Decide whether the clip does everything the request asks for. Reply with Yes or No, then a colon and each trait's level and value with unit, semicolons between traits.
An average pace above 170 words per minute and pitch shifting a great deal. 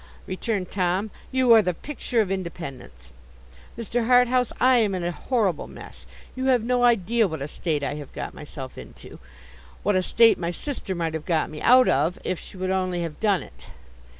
Yes: average, 190 wpm; wide, 6.1 semitones